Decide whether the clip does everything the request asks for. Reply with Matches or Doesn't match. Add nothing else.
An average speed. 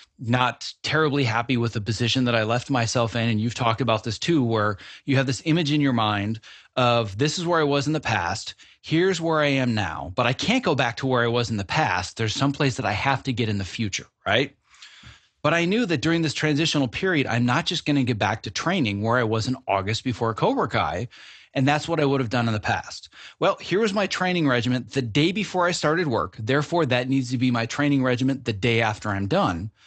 Doesn't match